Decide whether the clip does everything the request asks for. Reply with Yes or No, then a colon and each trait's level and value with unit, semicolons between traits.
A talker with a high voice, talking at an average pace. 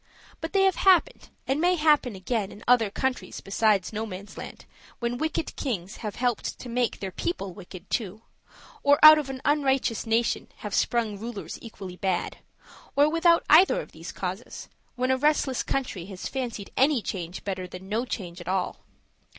Yes: high, 235 Hz; average, 170 wpm